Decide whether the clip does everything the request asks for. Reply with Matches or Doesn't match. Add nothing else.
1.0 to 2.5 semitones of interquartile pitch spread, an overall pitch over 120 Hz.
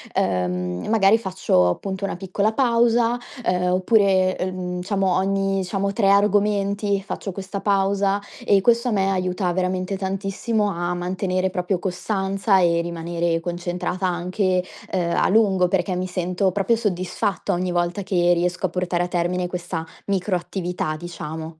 Matches